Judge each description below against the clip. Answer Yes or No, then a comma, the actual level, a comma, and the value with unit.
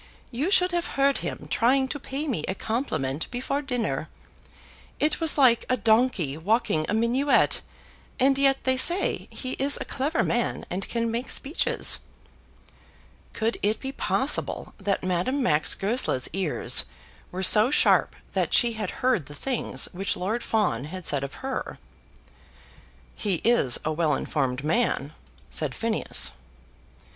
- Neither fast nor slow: Yes, average, 150 wpm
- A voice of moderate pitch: No, high, 230 Hz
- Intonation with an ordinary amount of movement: No, wide, 6.7 semitones